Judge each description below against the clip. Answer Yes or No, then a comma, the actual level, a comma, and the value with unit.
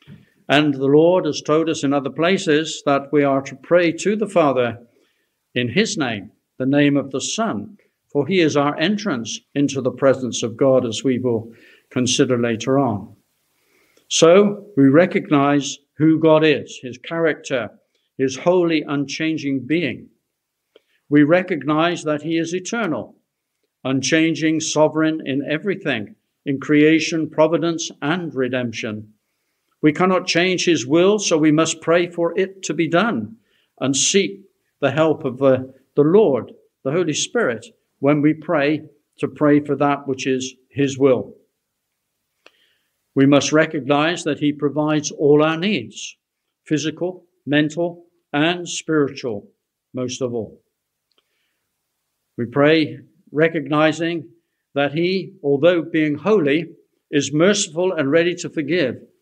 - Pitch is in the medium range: Yes, medium, 150 Hz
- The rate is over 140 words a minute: No, slow, 135 wpm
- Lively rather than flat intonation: No, average, 3.3 semitones